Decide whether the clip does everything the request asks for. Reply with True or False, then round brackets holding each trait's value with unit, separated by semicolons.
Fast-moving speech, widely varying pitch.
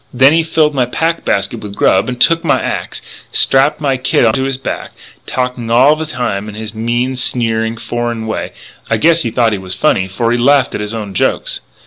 False (230 wpm; 3.4 semitones)